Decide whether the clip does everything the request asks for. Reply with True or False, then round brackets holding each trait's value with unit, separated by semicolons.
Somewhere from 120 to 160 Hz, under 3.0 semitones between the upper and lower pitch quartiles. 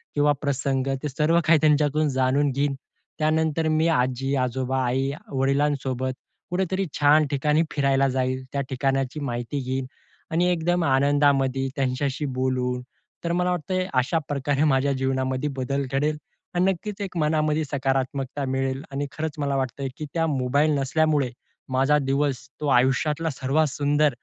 True (140 Hz; 2.5 semitones)